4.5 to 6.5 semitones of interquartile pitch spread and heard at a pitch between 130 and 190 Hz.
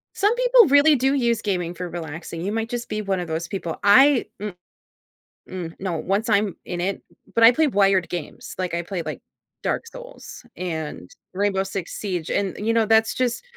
No: average, 5.0 semitones; high, 200 Hz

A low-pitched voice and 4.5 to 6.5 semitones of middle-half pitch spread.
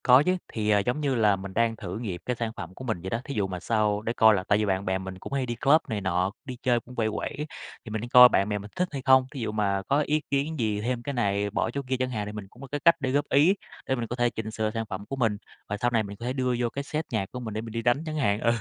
No: low, 115 Hz; average, 3.9 semitones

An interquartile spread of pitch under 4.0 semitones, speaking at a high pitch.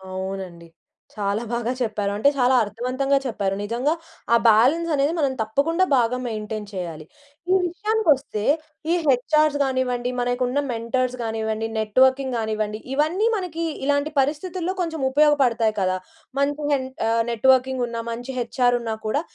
No: average, 4.4 semitones; very high, 250 Hz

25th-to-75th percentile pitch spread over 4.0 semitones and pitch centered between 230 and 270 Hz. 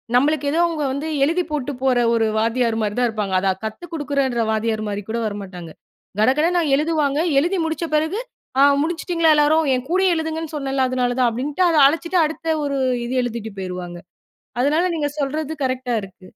No: wide, 5.6 semitones; very high, 280 Hz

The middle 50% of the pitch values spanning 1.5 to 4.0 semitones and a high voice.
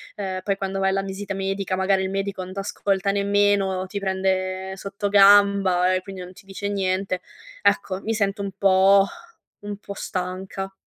No: narrow, 1.0 semitones; high, 195 Hz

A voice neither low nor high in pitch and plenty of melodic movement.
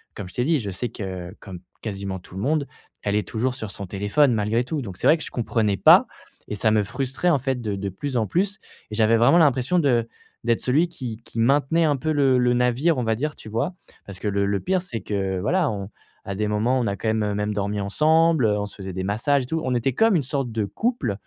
No: low, 115 Hz; wide, 5.7 semitones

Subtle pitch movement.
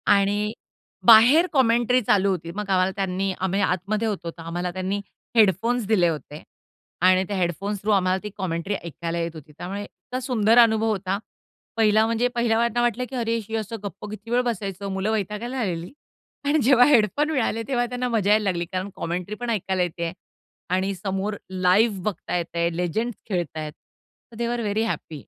No: average, 3.8 semitones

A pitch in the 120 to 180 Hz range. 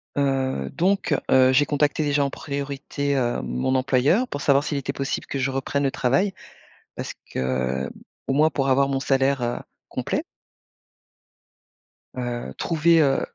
Yes: low, 135 Hz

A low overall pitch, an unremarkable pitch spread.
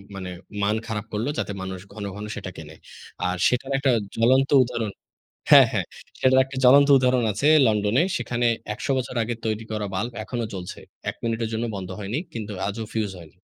Yes: low, 110 Hz; average, 3.5 semitones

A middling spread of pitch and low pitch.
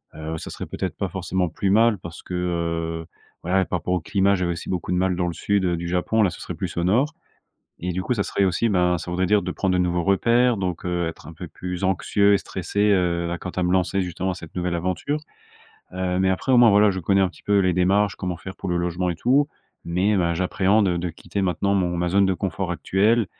No: narrow, 2.1 semitones; very low, 90 Hz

